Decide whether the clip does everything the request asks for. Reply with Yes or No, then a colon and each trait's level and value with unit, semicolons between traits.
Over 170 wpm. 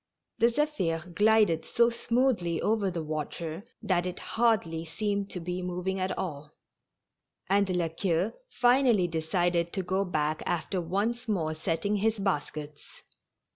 No: slow, 135 wpm